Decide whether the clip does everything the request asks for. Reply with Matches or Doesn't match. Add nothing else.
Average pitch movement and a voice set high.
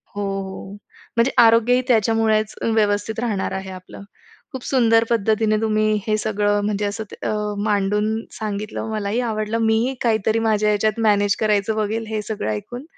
Doesn't match